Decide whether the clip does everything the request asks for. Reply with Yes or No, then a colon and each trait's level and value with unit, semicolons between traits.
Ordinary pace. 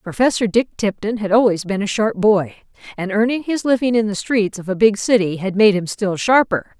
No: fast, 220 wpm